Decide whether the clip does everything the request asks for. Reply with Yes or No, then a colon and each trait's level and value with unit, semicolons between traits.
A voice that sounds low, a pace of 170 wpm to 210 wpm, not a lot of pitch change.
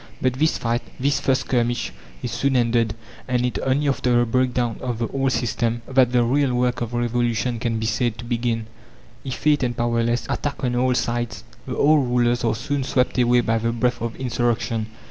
Yes: low, 120 Hz; average, 195 wpm; narrow, 1.5 semitones